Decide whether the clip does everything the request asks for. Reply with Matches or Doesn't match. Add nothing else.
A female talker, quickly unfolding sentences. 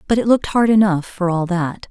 Matches